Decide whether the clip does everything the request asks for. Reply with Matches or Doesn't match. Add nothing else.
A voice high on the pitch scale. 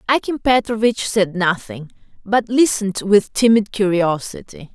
Matches